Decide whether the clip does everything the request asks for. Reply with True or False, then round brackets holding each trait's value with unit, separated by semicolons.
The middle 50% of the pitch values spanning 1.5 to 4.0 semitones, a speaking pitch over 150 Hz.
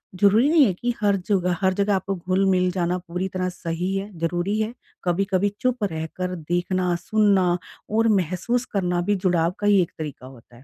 True (2.5 semitones; 185 Hz)